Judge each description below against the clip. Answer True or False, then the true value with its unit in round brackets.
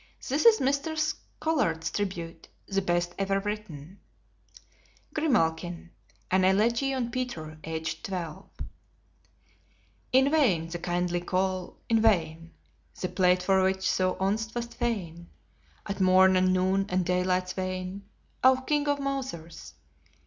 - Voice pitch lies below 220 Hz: True (190 Hz)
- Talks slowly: True (125 wpm)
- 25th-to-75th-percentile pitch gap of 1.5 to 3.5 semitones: False (5.0 semitones)